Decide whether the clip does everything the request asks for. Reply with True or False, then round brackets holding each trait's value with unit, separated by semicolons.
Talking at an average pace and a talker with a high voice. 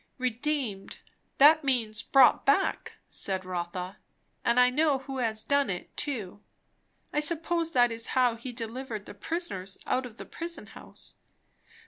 True (145 wpm; 250 Hz)